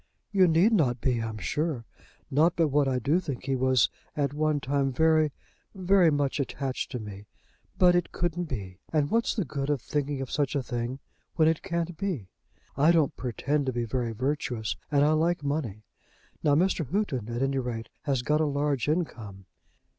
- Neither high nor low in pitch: Yes, medium, 145 Hz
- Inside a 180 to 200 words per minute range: Yes, average, 190 wpm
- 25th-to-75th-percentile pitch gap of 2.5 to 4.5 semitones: Yes, average, 4.1 semitones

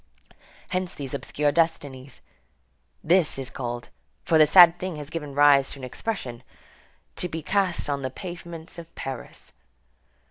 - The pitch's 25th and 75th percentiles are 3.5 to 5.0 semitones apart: Yes, average, 4.0 semitones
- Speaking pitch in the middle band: Yes, medium, 150 Hz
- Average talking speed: Yes, average, 145 wpm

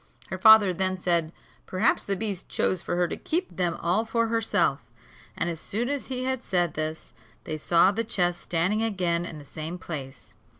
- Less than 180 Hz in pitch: No, medium, 185 Hz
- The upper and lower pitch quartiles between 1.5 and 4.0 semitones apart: No, average, 4.7 semitones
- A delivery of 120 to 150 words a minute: No, average, 195 wpm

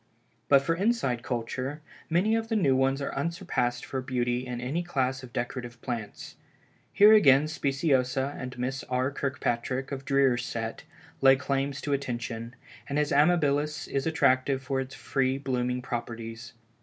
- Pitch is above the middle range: No, low, 135 Hz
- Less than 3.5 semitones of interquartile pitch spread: Yes, narrow, 2.4 semitones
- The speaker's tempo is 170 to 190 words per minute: No, average, 155 wpm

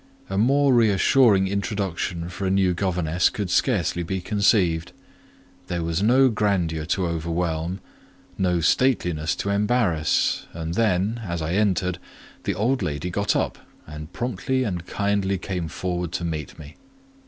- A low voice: Yes, very low, 95 Hz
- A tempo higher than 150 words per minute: No, average, 140 wpm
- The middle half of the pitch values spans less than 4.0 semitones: Yes, average, 3.4 semitones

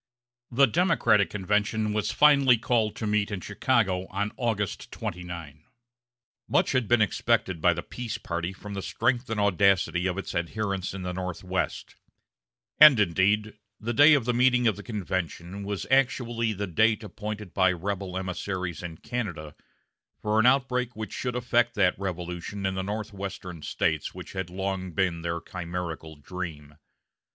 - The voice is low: Yes, low, 100 Hz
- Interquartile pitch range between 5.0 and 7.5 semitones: No, average, 3.7 semitones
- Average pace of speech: Yes, average, 155 wpm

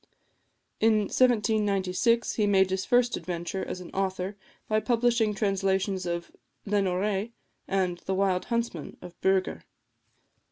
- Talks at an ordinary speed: No, slow, 120 wpm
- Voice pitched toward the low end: No, high, 195 Hz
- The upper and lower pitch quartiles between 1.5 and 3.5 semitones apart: Yes, narrow, 2.6 semitones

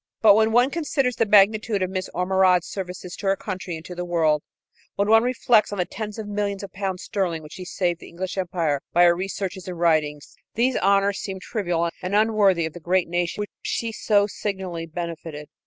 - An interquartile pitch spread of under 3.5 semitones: Yes, average, 3.0 semitones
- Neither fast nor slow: No, fast, 210 wpm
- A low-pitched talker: No, high, 190 Hz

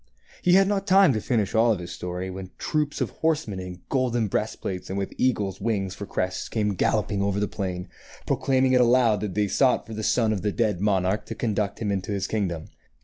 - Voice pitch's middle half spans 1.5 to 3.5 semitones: No, average, 4.3 semitones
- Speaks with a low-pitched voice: Yes, low, 105 Hz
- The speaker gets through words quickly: Yes, fast, 215 wpm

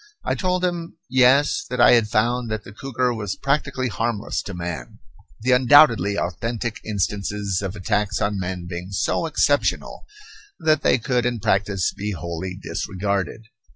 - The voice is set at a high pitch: No, low, 105 Hz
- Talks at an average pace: Yes, average, 155 wpm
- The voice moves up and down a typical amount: Yes, average, 4.6 semitones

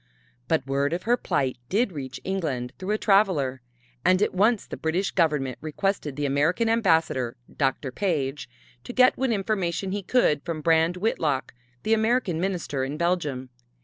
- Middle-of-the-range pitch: Yes, medium, 170 Hz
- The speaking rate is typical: Yes, average, 160 wpm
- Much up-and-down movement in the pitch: Yes, wide, 5.9 semitones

